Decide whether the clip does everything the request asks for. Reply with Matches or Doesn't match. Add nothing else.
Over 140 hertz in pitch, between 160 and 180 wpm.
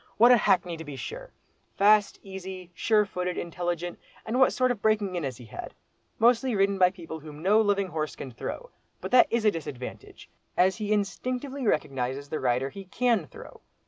Matches